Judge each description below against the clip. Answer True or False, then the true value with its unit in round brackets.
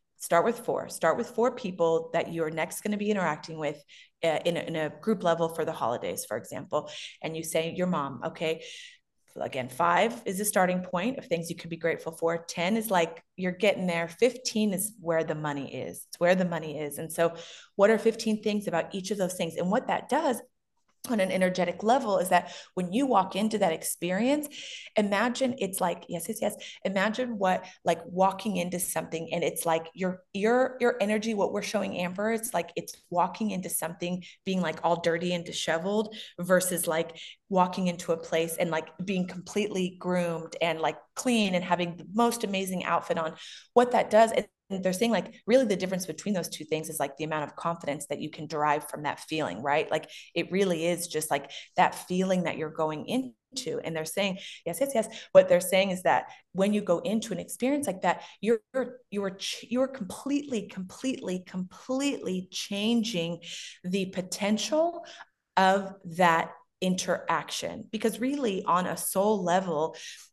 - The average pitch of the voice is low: False (185 Hz)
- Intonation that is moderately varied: True (4.3 semitones)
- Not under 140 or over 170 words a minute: False (195 wpm)